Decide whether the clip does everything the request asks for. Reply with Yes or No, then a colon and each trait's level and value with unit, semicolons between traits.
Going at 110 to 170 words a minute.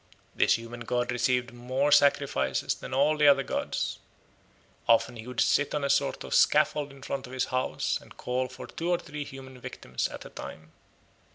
No: average, 190 wpm